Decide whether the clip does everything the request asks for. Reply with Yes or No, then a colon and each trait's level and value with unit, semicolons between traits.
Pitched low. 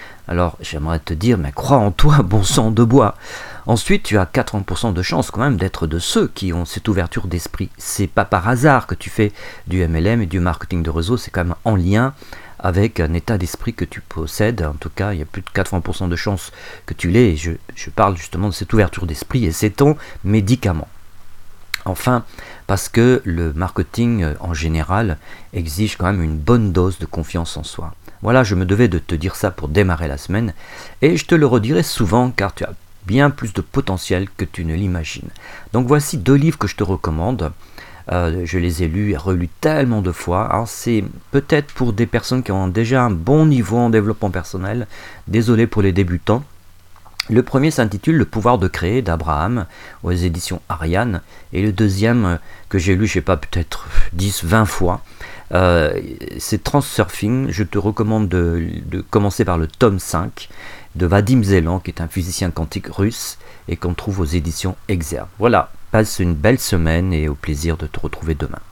Yes: very low, 95 Hz